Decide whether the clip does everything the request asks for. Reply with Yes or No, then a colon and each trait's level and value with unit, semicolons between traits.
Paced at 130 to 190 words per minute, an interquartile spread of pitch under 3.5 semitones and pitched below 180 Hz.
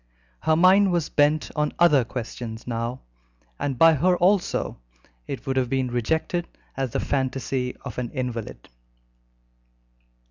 No: slow, 135 wpm; average, 4.5 semitones; low, 135 Hz